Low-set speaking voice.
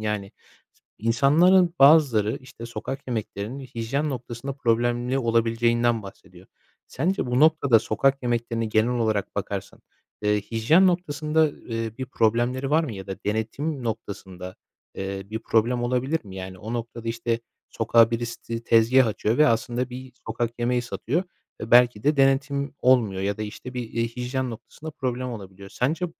Yes: low, 120 Hz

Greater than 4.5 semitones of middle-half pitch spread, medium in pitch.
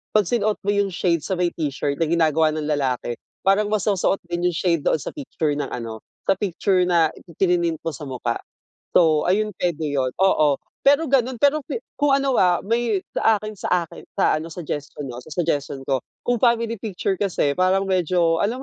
Yes: wide, 5.5 semitones; medium, 180 Hz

